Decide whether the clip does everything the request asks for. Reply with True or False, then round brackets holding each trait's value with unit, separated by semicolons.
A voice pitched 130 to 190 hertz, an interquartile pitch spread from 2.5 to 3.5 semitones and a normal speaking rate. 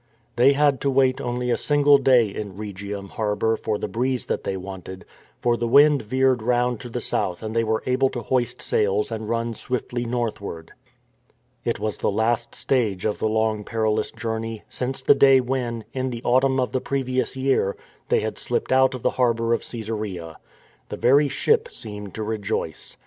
False (115 Hz; 3.2 semitones; 185 wpm)